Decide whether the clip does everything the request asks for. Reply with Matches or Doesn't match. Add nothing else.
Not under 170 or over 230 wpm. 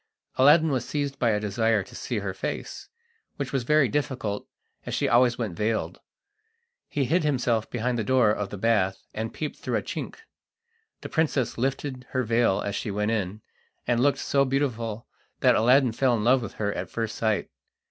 Matches